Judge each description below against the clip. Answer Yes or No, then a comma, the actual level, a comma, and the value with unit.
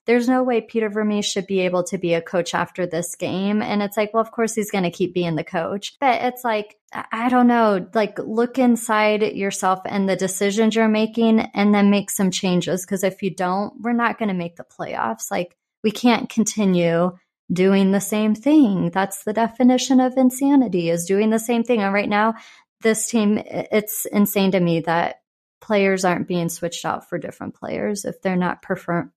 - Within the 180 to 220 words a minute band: Yes, fast, 205 wpm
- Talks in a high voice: Yes, high, 205 Hz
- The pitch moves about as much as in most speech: Yes, average, 3.6 semitones